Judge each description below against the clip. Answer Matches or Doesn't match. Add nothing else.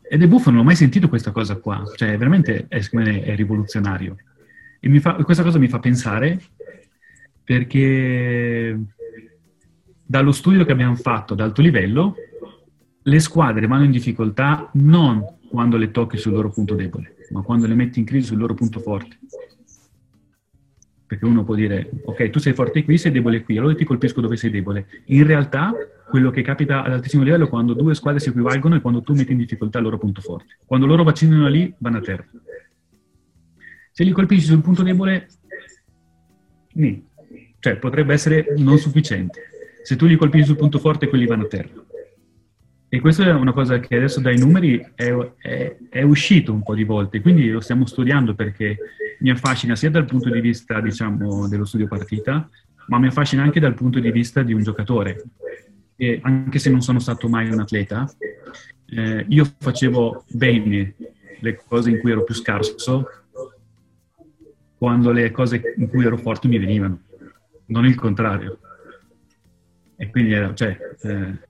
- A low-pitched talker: Matches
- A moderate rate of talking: Doesn't match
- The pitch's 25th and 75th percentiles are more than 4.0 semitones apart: Matches